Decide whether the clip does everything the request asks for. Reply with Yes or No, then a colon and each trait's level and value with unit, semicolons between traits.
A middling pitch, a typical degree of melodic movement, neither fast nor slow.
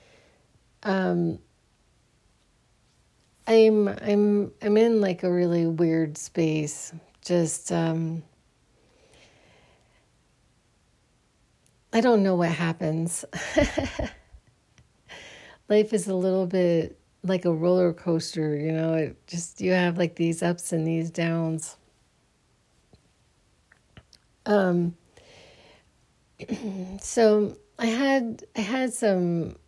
No: medium, 180 Hz; average, 4.0 semitones; slow, 90 wpm